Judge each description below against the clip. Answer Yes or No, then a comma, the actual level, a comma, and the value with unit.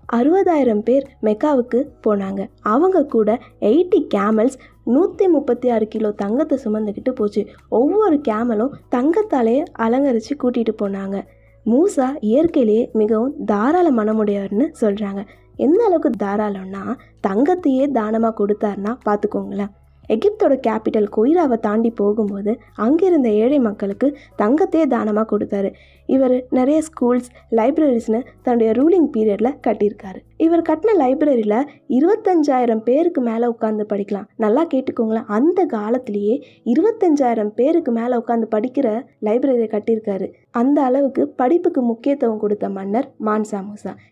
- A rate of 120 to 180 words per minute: No, average, 110 wpm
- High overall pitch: Yes, high, 235 Hz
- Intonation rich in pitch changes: No, average, 4.7 semitones